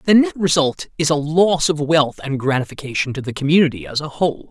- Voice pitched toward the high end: No, medium, 150 Hz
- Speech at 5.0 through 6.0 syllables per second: Yes, 5.9 syllables/s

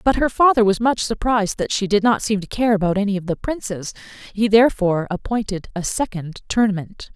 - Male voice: No, female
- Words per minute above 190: Yes, average, 200 wpm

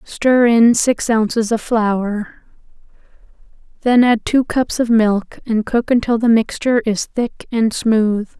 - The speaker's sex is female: Yes, female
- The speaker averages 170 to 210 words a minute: No, average, 150 wpm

